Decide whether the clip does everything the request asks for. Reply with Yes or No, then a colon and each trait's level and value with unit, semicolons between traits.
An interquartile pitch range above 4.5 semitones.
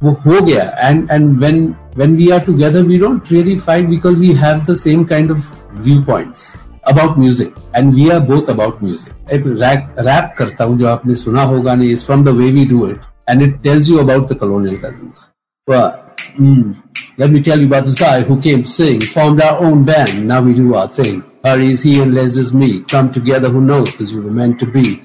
No: average, 3.5 semitones